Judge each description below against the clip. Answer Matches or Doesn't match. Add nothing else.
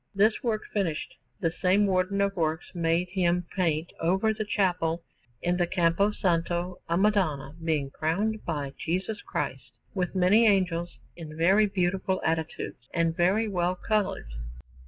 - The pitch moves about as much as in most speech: Matches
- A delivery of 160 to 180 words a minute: Doesn't match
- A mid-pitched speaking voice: Matches